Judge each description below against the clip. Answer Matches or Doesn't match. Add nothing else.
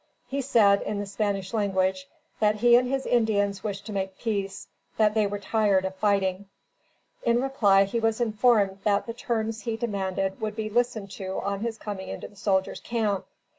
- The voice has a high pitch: Matches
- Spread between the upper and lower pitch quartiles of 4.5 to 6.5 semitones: Doesn't match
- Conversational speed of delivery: Matches